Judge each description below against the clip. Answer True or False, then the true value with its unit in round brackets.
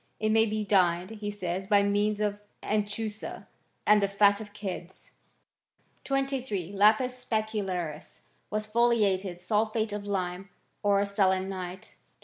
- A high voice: True (205 Hz)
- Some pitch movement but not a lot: False (2.1 semitones)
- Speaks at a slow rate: True (125 wpm)